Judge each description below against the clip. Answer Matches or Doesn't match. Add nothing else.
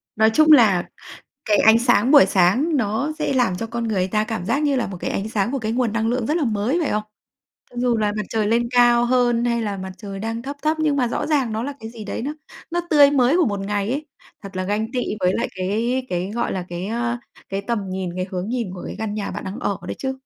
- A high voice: Matches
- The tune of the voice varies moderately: Matches